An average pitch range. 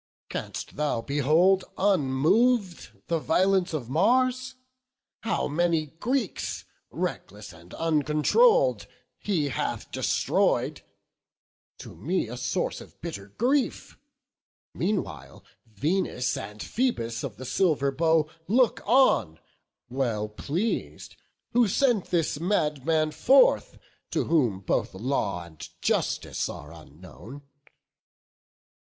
No: wide, 8.6 semitones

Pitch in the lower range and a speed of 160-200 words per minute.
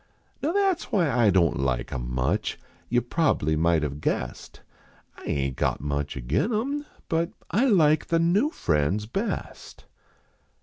Yes: low, 105 Hz; average, 165 wpm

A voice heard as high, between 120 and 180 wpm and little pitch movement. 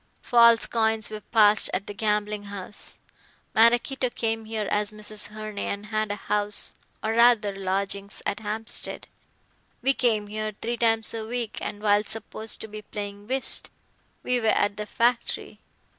Yes: high, 215 Hz; average, 160 wpm; narrow, 1.5 semitones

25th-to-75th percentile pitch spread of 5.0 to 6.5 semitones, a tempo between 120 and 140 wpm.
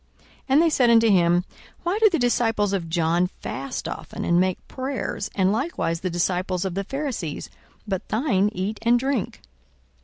No: wide, 5.6 semitones; average, 175 wpm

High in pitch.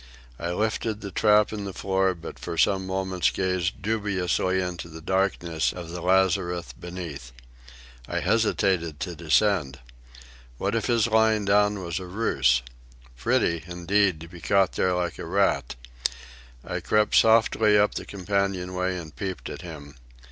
No: very low, 95 Hz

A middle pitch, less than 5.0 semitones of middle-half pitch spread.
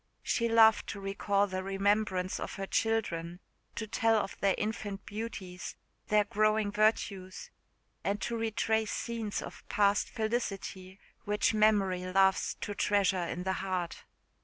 No: high, 205 Hz; narrow, 2.4 semitones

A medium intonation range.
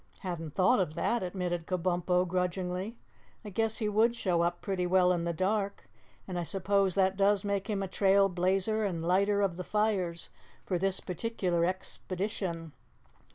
No: narrow, 2.1 semitones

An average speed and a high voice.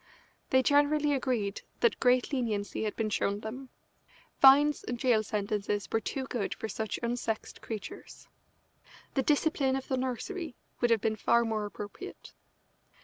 Yes: average, 145 wpm; high, 240 Hz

